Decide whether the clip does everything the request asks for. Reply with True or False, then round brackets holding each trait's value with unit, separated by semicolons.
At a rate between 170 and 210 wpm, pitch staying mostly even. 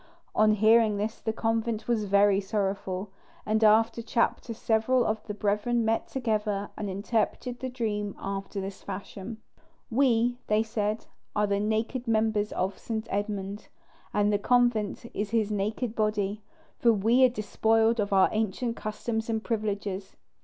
False (150 wpm; 1.9 semitones)